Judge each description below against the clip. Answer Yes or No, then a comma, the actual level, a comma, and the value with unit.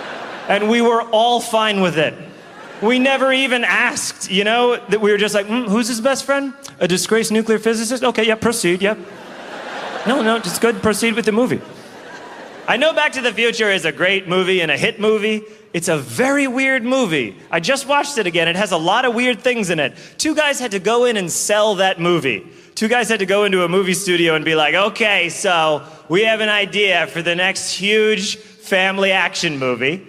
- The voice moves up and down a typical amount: Yes, average, 4.2 semitones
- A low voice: No, high, 215 Hz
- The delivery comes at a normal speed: No, fast, 215 wpm